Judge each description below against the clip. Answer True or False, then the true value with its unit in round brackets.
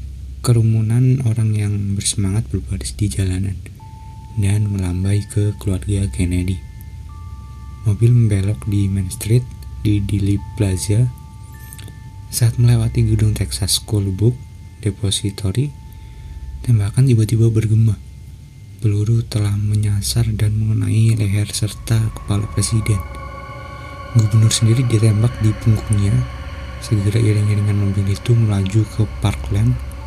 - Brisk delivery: False (100 wpm)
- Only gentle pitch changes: True (2.2 semitones)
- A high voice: False (105 Hz)